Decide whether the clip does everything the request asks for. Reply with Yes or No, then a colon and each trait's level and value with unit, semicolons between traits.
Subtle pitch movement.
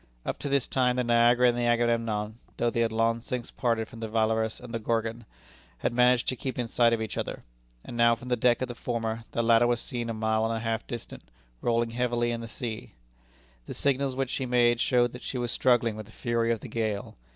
Yes: narrow, 1.3 semitones